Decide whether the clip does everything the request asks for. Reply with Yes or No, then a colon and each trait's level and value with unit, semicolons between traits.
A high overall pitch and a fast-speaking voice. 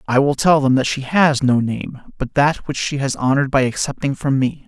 No: low, 135 Hz; fast, 245 wpm